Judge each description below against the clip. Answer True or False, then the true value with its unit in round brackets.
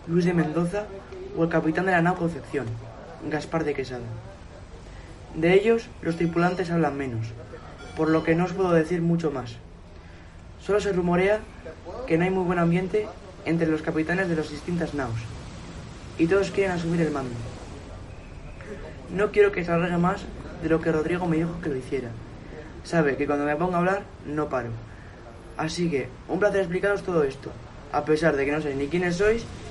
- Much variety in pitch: True (6.6 semitones)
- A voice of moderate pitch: True (160 Hz)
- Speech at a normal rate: True (180 wpm)